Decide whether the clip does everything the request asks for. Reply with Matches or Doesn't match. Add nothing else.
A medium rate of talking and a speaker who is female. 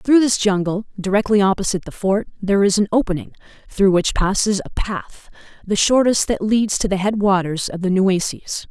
Matches